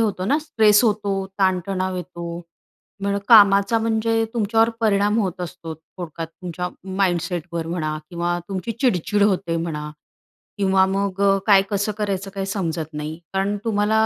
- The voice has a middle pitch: No, high, 195 Hz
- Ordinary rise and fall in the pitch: Yes, average, 3.1 semitones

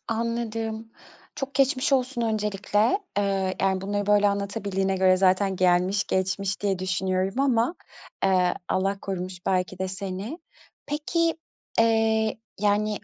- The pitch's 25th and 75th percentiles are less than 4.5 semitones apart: Yes, average, 3.2 semitones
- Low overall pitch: No, high, 200 Hz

